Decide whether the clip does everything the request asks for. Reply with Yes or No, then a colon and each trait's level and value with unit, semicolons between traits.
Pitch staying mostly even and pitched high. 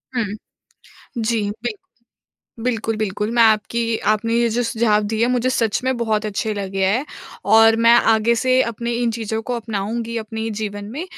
Yes: narrow, 1.7 semitones; high, 225 Hz